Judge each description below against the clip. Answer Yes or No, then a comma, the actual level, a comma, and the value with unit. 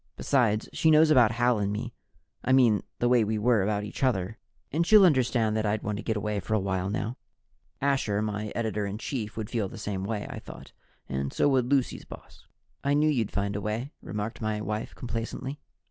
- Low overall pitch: Yes, low, 110 Hz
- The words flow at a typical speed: No, fast, 210 wpm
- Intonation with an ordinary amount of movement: Yes, average, 3.3 semitones